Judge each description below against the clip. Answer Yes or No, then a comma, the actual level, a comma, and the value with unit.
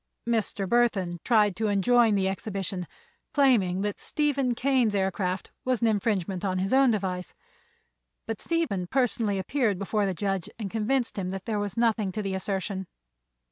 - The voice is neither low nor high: No, high, 205 Hz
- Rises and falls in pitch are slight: No, average, 3.7 semitones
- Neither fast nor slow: Yes, average, 155 wpm